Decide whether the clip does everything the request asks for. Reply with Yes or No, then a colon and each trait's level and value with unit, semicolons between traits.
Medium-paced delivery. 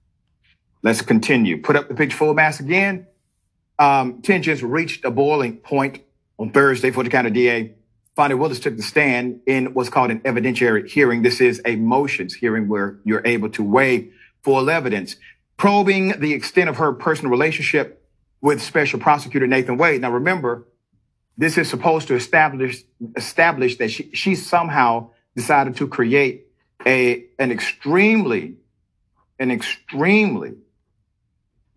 Yes: average, 145 wpm